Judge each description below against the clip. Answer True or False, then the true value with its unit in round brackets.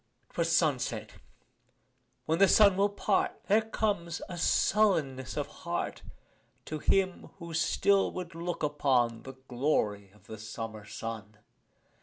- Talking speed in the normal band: False (130 wpm)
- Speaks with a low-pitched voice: False (155 Hz)